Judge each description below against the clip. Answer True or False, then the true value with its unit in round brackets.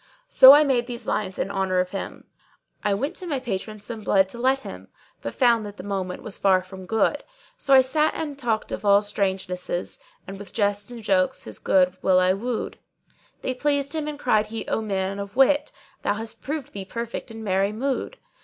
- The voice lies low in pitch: False (215 Hz)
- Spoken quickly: True (220 wpm)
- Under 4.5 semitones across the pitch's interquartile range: False (5.0 semitones)